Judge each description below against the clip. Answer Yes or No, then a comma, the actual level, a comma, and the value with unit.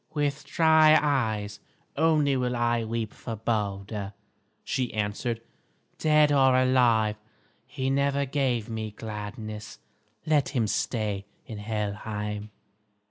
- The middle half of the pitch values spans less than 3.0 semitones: No, average, 4.5 semitones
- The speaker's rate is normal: No, slow, 110 wpm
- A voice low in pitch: Yes, low, 115 Hz